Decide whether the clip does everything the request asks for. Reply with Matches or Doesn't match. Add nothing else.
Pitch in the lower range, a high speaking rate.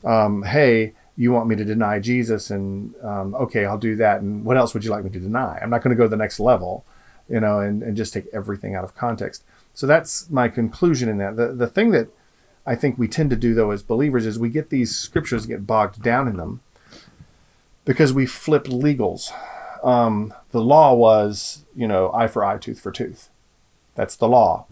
Matches